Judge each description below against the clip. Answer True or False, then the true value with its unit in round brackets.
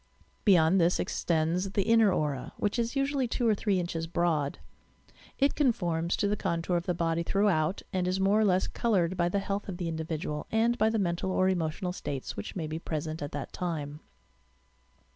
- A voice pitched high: False (180 Hz)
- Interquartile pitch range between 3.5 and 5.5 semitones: True (3.8 semitones)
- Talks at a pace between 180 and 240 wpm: True (200 wpm)